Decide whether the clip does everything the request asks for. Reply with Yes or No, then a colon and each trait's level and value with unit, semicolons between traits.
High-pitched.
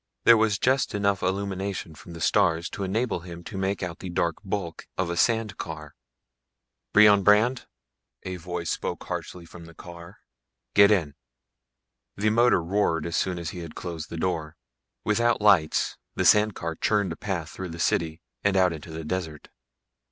No: very low, 90 Hz